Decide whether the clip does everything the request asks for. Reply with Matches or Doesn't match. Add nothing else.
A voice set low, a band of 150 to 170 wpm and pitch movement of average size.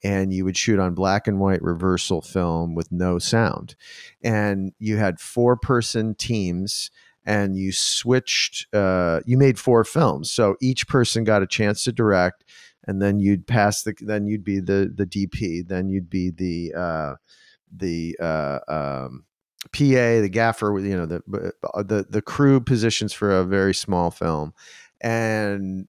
Matches